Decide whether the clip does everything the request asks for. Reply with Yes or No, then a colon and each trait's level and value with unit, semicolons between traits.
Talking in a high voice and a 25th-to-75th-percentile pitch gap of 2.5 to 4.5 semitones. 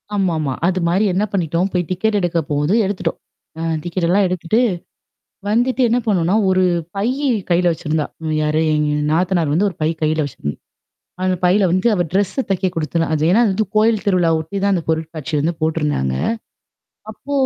No: medium, 175 Hz; average, 3.9 semitones